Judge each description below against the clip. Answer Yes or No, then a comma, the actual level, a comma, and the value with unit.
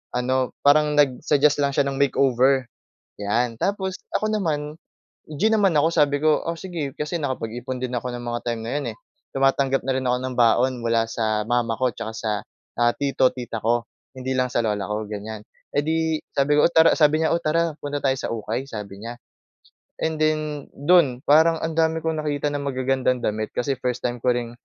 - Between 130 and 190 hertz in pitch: Yes, low, 135 Hz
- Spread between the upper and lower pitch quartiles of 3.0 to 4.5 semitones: Yes, average, 3.8 semitones